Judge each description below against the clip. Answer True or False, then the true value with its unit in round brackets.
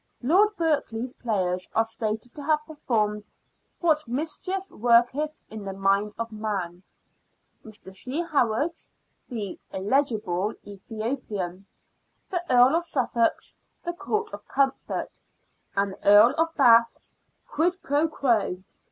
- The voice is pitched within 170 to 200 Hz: False (235 Hz)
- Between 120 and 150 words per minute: True (145 wpm)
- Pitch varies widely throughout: True (6.5 semitones)